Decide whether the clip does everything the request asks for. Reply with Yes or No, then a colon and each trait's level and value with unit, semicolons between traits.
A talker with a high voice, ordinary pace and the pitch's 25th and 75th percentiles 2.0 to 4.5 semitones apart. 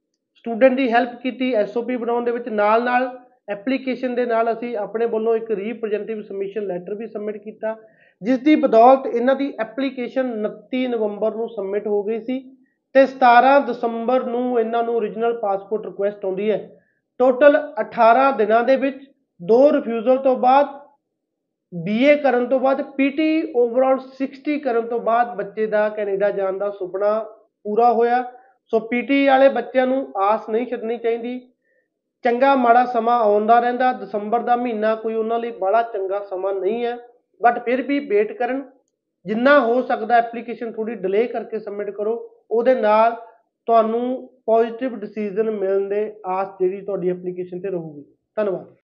Yes: high, 235 Hz; average, 155 wpm; average, 3.3 semitones